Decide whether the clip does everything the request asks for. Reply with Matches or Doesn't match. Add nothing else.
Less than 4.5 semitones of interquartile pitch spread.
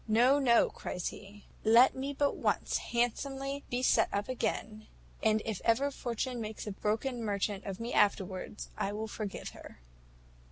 Matches